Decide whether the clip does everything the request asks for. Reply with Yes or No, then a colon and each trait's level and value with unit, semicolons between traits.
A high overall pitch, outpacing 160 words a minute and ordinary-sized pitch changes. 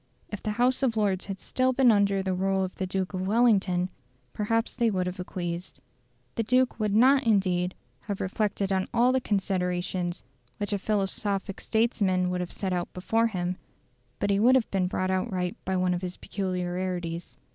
Yes: high, 195 Hz; average, 185 wpm; average, 3.0 semitones